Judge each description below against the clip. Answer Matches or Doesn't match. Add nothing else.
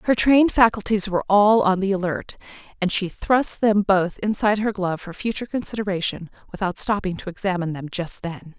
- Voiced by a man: Doesn't match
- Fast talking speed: Doesn't match